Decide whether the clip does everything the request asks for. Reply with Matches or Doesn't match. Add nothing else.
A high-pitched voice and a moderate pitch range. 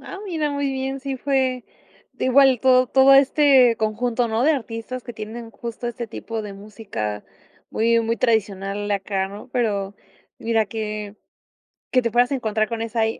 Matches